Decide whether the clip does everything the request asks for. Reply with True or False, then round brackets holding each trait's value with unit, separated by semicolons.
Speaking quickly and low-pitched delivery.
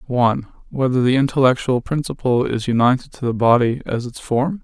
False (170 wpm; 125 Hz)